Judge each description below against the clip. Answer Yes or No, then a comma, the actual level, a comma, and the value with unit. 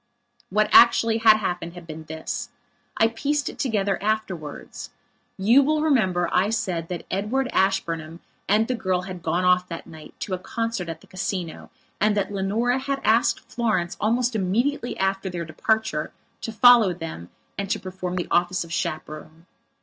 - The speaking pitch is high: Yes, high, 195 Hz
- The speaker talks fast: No, average, 165 wpm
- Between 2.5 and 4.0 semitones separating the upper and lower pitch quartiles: No, average, 4.5 semitones